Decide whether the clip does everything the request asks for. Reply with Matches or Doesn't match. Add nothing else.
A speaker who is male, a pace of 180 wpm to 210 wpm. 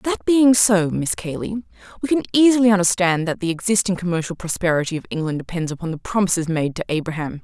Doesn't match